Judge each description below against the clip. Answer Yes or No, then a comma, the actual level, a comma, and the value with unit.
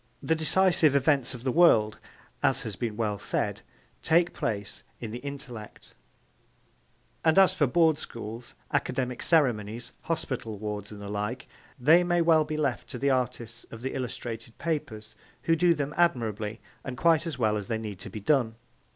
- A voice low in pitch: Yes, low, 125 Hz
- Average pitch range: No, wide, 6.1 semitones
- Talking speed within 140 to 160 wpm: No, average, 170 wpm